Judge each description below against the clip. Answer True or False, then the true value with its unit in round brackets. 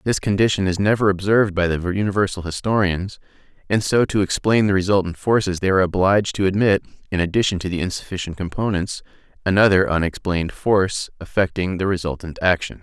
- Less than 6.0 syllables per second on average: False (6.1 syllables/s)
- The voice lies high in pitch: False (95 Hz)